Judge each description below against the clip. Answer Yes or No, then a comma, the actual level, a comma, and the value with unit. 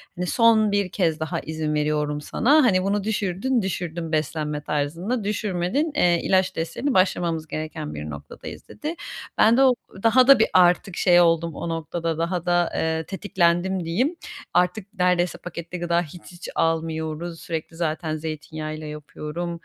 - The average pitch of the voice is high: No, medium, 175 Hz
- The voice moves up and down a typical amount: Yes, average, 3.3 semitones